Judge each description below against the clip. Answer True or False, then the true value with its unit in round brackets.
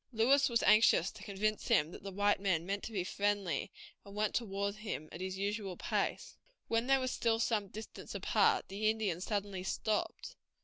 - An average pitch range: False (2.3 semitones)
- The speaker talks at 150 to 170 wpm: False (185 wpm)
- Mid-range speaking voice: False (205 Hz)